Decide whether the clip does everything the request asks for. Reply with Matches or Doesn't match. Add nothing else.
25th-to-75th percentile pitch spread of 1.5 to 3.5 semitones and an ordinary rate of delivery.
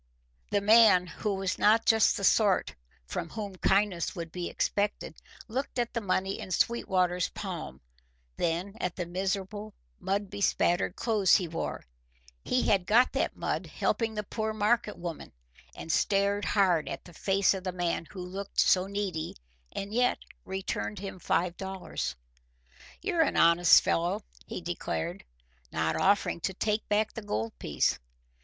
Matches